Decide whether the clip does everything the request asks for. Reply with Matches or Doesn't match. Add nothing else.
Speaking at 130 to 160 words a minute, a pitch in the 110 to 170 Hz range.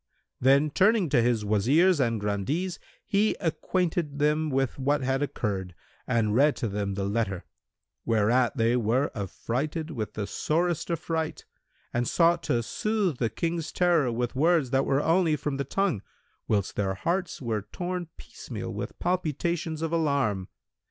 Matches